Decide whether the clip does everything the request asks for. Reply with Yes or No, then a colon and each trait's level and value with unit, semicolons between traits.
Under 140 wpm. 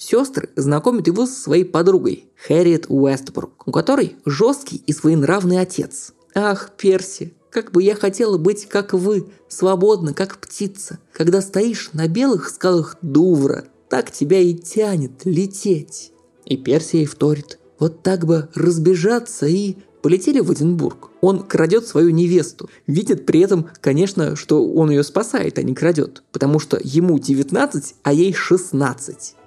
No: average, 145 wpm